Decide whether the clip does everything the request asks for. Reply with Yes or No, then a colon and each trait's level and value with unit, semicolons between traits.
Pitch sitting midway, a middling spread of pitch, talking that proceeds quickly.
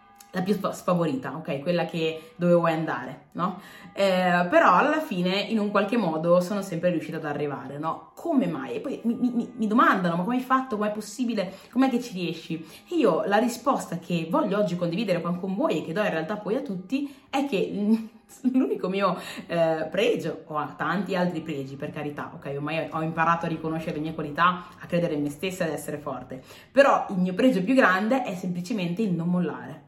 Yes: medium, 180 Hz; average, 5.0 semitones; fast, 205 wpm